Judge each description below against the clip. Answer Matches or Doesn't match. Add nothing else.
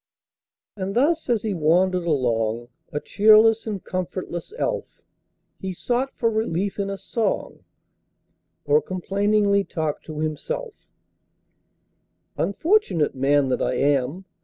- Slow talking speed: Matches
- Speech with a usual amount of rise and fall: Doesn't match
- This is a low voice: Doesn't match